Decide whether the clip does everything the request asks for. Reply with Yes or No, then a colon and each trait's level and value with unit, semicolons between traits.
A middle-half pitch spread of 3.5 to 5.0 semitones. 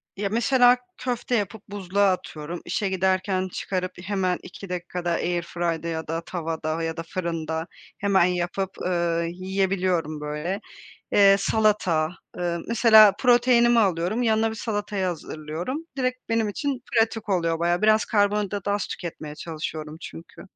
Yes: average, 3.9 semitones